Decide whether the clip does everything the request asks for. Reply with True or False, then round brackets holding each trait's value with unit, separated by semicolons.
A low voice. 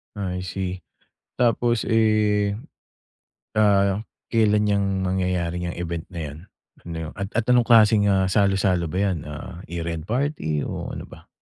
True (95 Hz)